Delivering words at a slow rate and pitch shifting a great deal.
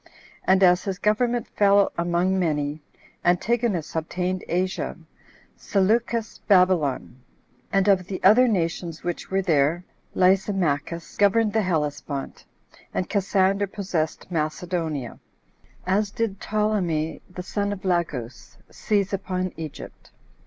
No: slow, 110 wpm; average, 3.3 semitones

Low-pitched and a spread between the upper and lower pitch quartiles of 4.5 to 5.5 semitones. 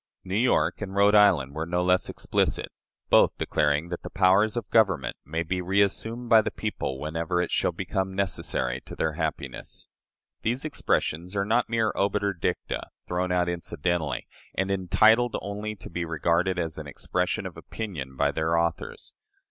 No: very low, 90 Hz; average, 3.8 semitones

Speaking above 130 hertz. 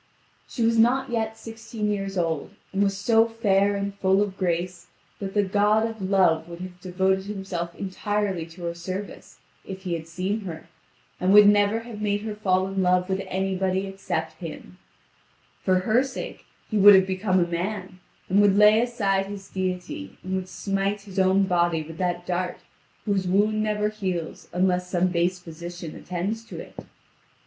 Yes: high, 190 Hz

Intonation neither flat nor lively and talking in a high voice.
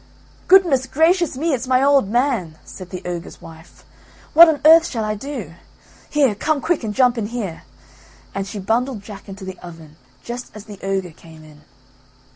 No: wide, 6.6 semitones; high, 225 Hz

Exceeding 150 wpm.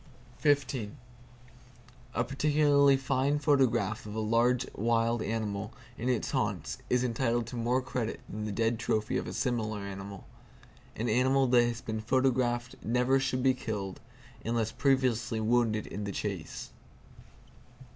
No: slow, 135 wpm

